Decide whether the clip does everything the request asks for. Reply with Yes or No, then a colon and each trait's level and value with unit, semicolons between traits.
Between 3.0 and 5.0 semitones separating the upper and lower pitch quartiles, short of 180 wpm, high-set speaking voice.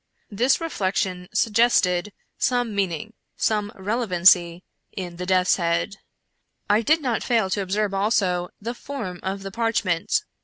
Yes: average, 3.9 semitones; average, 150 wpm; high, 195 Hz